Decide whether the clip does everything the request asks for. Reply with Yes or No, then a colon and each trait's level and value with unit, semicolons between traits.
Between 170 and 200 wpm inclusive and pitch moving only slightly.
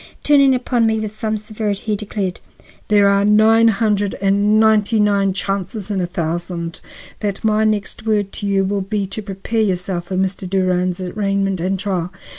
Yes: average, 175 wpm; narrow, 2.1 semitones